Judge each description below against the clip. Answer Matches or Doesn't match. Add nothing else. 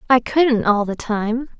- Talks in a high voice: Matches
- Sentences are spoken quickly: Doesn't match